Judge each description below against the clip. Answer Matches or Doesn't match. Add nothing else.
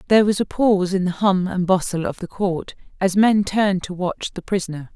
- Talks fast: Matches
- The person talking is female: Matches